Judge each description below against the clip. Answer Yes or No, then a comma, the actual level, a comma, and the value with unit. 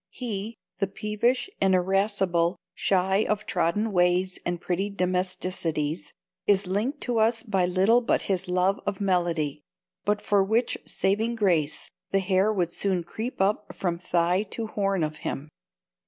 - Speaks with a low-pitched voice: No, high, 190 Hz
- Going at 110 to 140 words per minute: No, average, 150 wpm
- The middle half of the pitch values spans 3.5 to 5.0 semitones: No, average, 2.9 semitones